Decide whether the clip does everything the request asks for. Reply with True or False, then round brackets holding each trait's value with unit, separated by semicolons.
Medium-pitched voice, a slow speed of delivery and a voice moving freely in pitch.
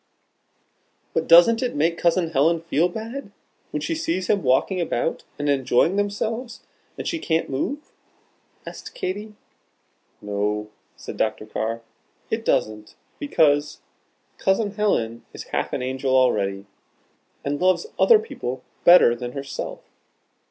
True (165 Hz; 130 wpm; 8.2 semitones)